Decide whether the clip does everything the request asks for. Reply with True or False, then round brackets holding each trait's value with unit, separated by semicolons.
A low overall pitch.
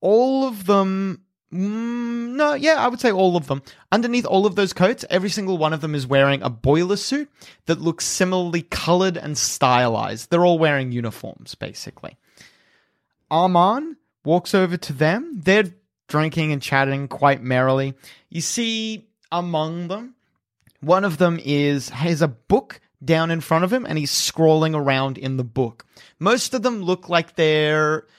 False (170 Hz)